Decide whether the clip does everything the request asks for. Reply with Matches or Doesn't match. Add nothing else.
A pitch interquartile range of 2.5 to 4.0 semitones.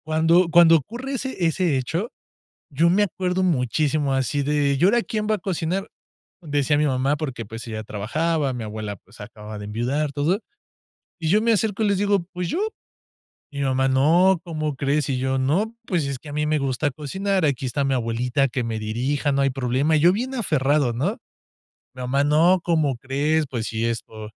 Doesn't match